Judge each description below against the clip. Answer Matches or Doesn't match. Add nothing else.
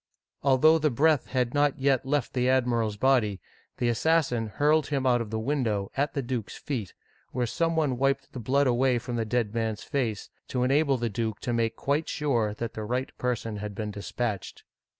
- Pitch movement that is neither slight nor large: Matches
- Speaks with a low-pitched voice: Matches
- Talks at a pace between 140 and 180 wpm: Doesn't match